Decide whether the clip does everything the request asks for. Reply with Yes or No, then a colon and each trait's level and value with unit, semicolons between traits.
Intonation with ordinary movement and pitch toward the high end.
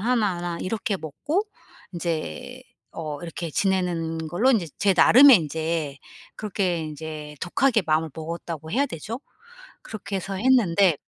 No: average, 4.8 semitones; medium, 175 Hz